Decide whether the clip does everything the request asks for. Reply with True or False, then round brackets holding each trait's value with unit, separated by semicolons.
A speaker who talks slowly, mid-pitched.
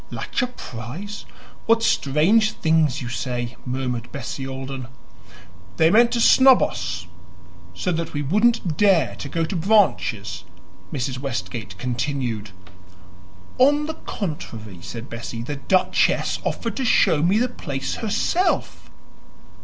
True (125 wpm; 145 Hz)